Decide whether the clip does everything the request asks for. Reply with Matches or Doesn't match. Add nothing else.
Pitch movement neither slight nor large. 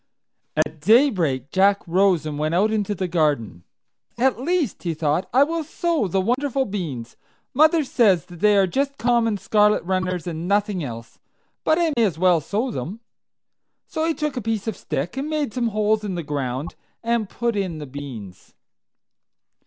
Doesn't match